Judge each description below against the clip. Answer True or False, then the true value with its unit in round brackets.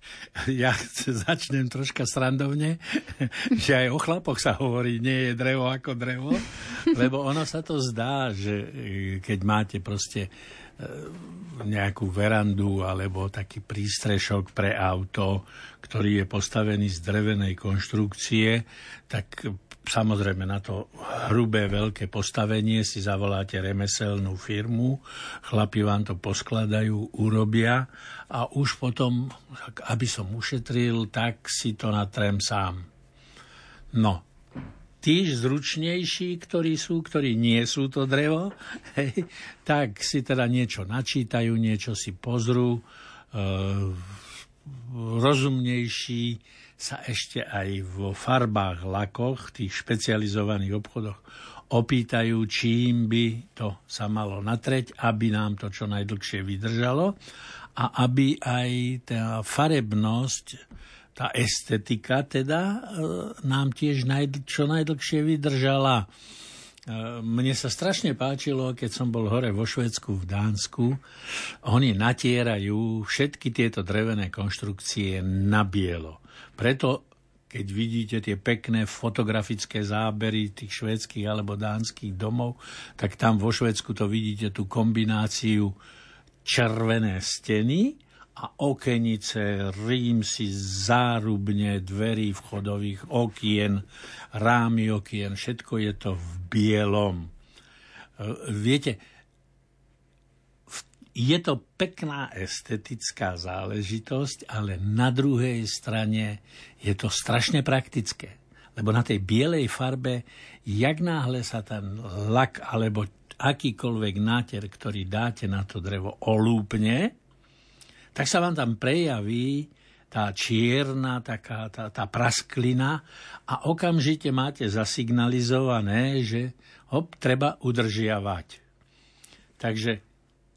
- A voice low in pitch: True (115 Hz)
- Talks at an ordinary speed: False (105 wpm)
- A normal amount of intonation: True (3.7 semitones)